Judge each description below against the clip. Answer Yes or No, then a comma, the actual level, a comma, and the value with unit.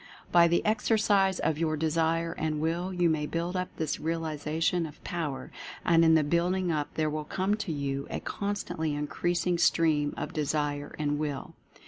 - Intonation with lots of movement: No, narrow, 2.5 semitones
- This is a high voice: No, medium, 160 Hz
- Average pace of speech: Yes, average, 170 wpm